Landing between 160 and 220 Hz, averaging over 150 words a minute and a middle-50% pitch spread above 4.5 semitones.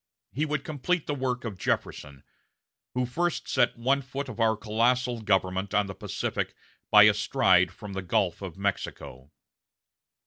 No: low, 110 Hz; average, 160 wpm; average, 5.2 semitones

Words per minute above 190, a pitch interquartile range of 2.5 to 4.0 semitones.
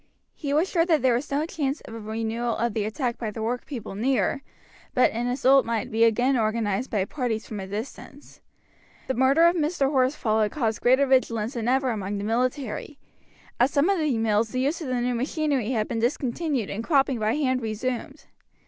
Yes: average, 200 wpm; average, 3.7 semitones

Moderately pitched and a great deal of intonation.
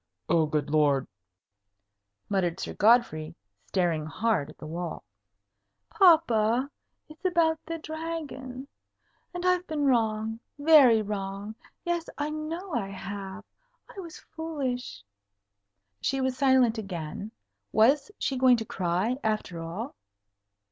No: high, 235 Hz; wide, 7.9 semitones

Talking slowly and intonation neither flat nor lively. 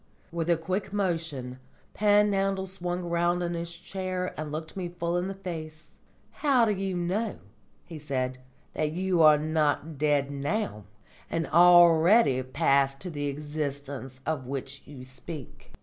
No: average, 150 wpm; average, 4.2 semitones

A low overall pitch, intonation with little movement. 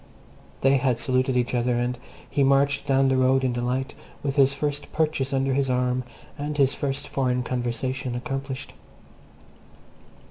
Yes: low, 130 Hz; narrow, 1.6 semitones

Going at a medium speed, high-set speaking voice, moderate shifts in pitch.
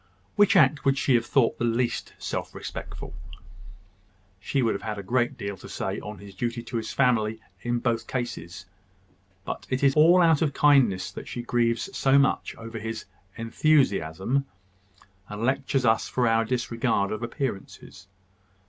No: average, 165 wpm; low, 120 Hz; average, 3.3 semitones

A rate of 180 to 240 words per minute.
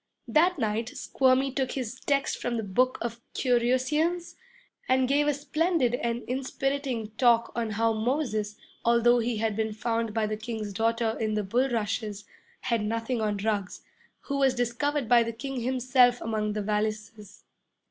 No: average, 155 wpm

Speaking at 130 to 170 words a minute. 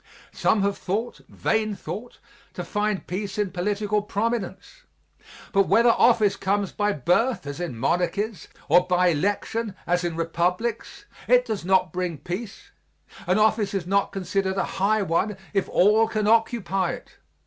Yes: average, 150 wpm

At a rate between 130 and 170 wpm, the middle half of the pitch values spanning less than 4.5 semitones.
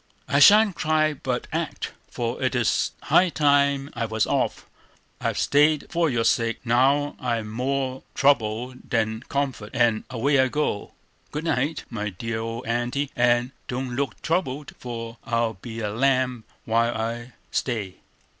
Yes: average, 150 wpm; average, 3.5 semitones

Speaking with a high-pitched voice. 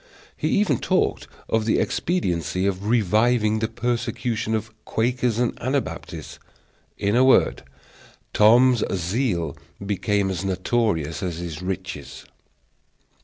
No: low, 110 Hz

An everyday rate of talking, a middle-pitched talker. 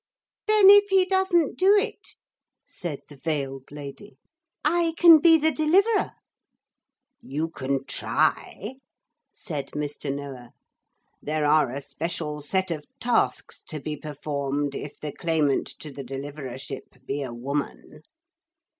No: slow, 130 wpm; medium, 150 Hz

